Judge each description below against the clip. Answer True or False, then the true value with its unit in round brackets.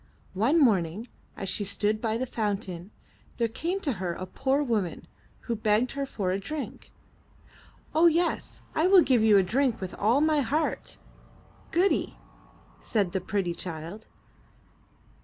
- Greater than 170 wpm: False (150 wpm)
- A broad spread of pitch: True (6.4 semitones)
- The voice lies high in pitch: True (220 Hz)